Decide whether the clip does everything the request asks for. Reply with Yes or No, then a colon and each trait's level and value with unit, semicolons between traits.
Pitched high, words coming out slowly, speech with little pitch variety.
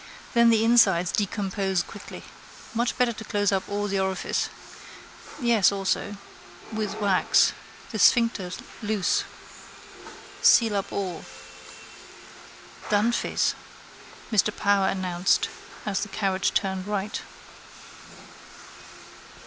Yes: high, 205 Hz; slow, 100 wpm; narrow, 2.2 semitones